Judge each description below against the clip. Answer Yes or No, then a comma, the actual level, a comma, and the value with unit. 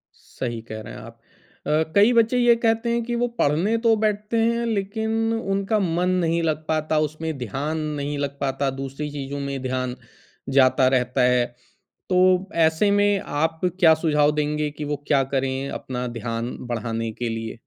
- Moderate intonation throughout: No, wide, 7.4 semitones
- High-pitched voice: No, medium, 150 Hz